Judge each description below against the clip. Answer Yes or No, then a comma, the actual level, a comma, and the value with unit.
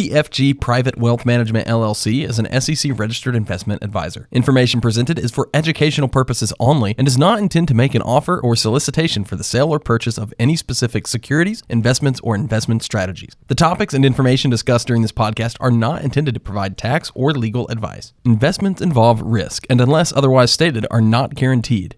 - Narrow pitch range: No, average, 3.5 semitones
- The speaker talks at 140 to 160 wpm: No, average, 185 wpm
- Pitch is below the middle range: Yes, low, 120 Hz